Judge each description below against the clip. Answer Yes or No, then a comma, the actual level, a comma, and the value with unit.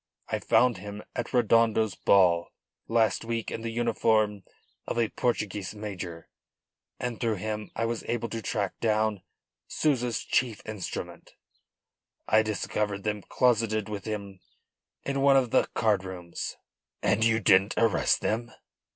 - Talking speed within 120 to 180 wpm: Yes, average, 140 wpm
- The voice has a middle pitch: No, low, 110 Hz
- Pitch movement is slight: Yes, narrow, 2.2 semitones